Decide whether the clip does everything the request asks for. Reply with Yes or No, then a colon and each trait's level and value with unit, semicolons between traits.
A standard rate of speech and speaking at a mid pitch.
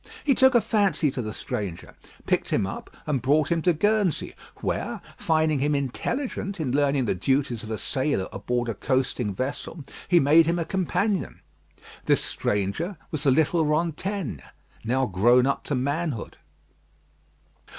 Yes: average, 155 wpm; medium, 145 Hz